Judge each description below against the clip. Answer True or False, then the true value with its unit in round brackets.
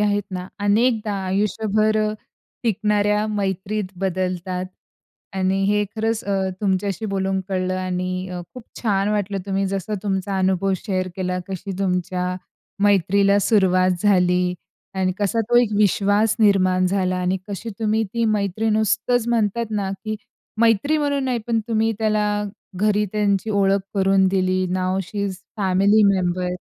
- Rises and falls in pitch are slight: True (2.3 semitones)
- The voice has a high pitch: True (200 Hz)